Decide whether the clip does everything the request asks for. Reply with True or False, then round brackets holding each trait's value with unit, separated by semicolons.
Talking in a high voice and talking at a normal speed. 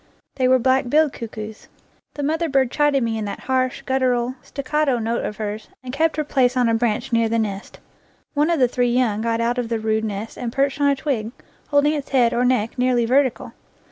False (250 Hz; 220 wpm)